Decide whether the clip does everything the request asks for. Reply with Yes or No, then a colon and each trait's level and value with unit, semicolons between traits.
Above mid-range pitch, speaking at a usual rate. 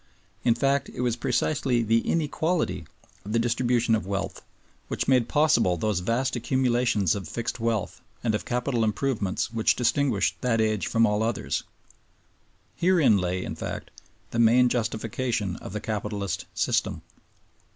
No: low, 115 Hz; average, 145 wpm